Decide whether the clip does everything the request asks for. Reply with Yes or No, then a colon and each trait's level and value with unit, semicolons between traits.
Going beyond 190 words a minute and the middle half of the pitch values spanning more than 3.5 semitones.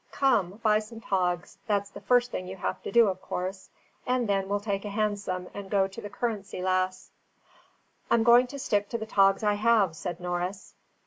No: average, 200 wpm; average, 2.8 semitones